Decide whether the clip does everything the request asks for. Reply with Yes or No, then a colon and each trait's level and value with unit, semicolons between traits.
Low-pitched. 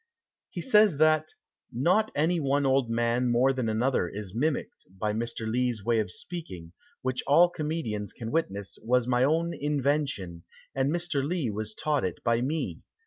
Yes: low, 130 Hz